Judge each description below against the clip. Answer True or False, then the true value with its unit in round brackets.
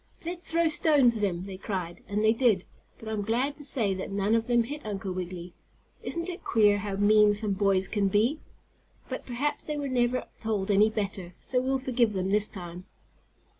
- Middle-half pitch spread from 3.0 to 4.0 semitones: False (4.6 semitones)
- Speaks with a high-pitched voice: True (215 Hz)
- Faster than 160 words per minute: True (200 wpm)